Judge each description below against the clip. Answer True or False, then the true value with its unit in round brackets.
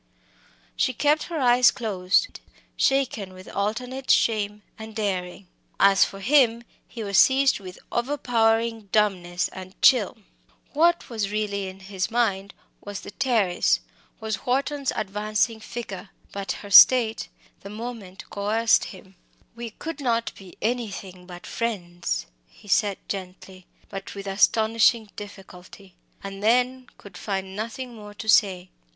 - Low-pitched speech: False (210 Hz)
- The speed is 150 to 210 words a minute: False (135 wpm)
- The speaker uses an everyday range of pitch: True (3.5 semitones)